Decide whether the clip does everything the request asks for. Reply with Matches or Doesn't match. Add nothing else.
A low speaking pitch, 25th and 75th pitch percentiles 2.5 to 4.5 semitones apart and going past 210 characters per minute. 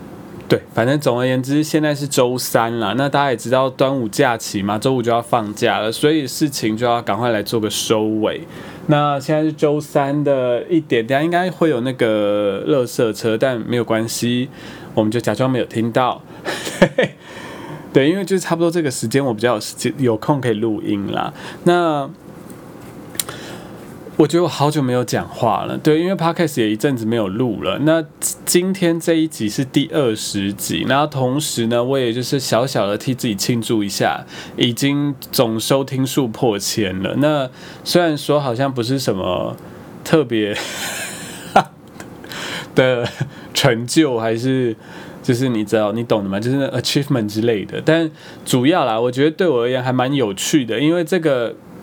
Doesn't match